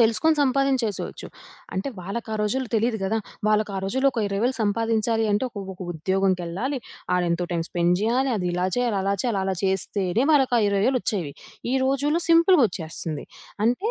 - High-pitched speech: Yes, high, 215 Hz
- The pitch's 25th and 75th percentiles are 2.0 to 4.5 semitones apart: No, average, 5.1 semitones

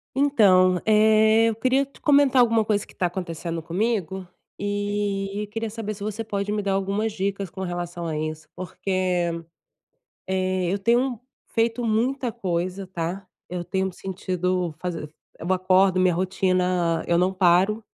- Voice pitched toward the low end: No, high, 190 Hz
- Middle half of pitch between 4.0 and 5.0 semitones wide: No, average, 3.2 semitones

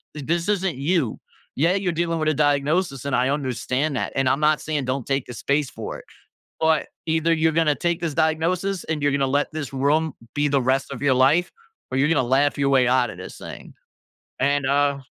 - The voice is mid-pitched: Yes, medium, 145 Hz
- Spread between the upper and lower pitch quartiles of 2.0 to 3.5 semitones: Yes, average, 2.9 semitones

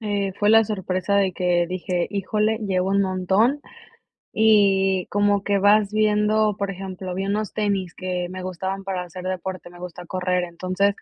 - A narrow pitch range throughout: Yes, narrow, 2.0 semitones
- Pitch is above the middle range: Yes, high, 195 Hz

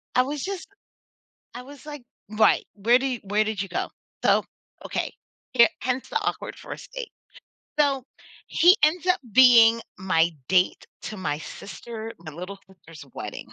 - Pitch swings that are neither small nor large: No, wide, 6.3 semitones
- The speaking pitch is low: No, high, 230 Hz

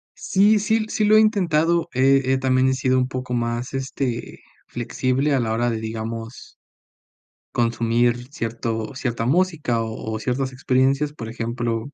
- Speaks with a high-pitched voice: No, low, 125 Hz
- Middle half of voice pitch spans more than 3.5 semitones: No, average, 3.0 semitones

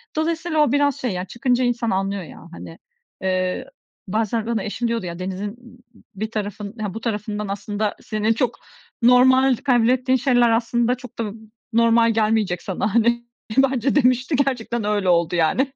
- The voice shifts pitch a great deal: No, average, 3.4 semitones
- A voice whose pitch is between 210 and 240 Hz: Yes, high, 230 Hz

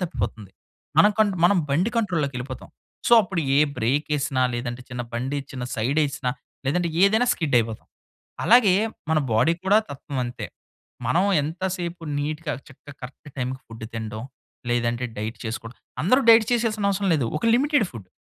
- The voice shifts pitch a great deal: Yes, wide, 6.9 semitones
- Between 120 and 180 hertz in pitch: Yes, medium, 140 Hz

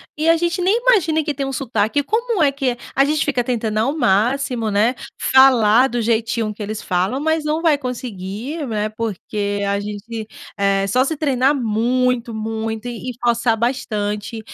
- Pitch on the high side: Yes, high, 240 Hz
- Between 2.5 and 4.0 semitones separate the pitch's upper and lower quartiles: No, average, 4.5 semitones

